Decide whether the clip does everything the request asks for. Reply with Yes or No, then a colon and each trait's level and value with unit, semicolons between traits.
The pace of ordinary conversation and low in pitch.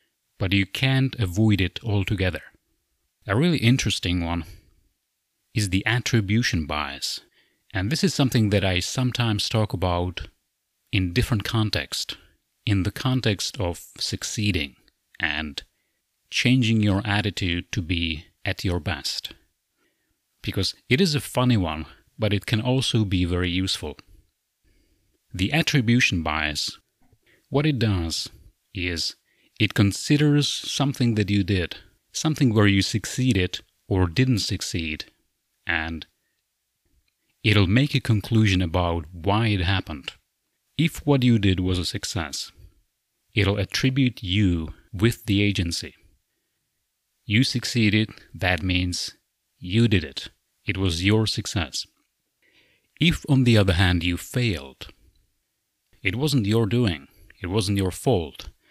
No: slow, 125 wpm; low, 100 Hz